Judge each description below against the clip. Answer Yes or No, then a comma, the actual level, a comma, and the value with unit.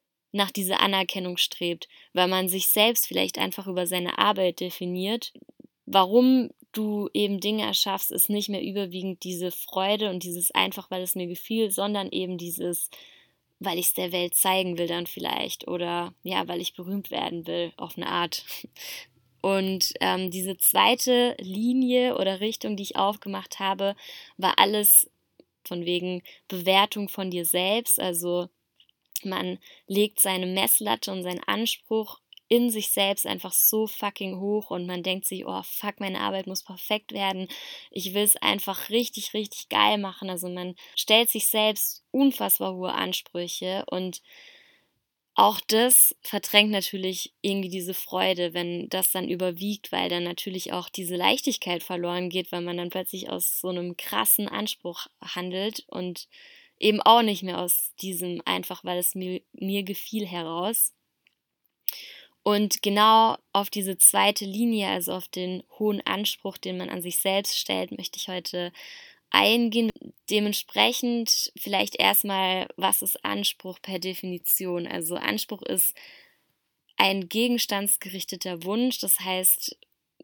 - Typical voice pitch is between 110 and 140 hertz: No, high, 190 Hz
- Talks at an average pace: Yes, average, 145 wpm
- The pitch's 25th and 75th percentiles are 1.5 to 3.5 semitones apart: Yes, average, 2.8 semitones